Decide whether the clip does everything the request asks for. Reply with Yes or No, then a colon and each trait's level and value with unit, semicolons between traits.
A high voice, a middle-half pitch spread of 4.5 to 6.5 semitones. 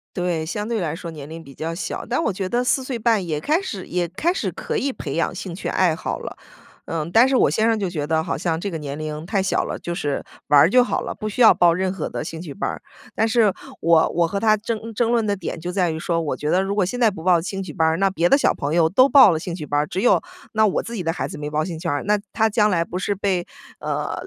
No: medium, 180 Hz; average, 4.9 semitones